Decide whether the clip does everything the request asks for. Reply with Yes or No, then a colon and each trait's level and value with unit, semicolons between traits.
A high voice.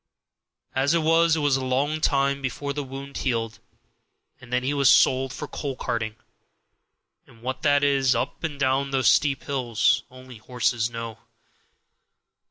No: low, 135 Hz